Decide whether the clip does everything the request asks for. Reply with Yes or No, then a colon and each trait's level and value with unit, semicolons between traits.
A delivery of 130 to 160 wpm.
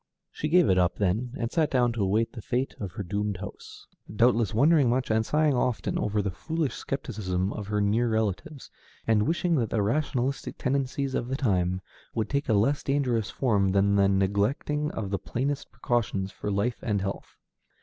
No: average, 190 wpm